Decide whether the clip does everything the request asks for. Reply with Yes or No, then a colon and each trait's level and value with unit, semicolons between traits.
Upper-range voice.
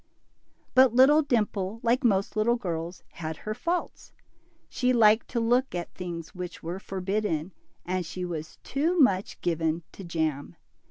Yes: high, 195 Hz